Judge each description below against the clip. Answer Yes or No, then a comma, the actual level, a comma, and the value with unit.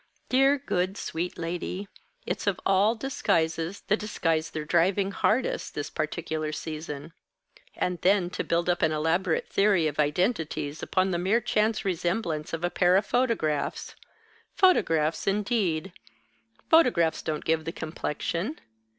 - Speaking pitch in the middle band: Yes, medium, 175 Hz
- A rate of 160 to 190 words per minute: No, slow, 135 wpm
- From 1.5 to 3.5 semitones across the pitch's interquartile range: No, average, 4.1 semitones